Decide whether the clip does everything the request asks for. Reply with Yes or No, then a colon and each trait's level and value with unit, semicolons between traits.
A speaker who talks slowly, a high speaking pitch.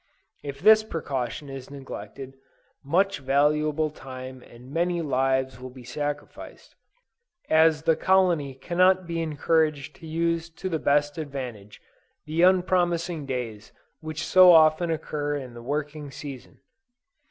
No: slow, 130 wpm; medium, 150 Hz